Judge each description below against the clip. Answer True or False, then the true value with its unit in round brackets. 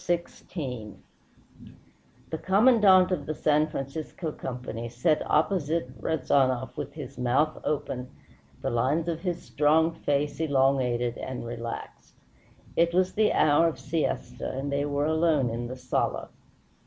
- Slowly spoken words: True (130 wpm)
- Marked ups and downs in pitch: False (4.2 semitones)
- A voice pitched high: False (145 Hz)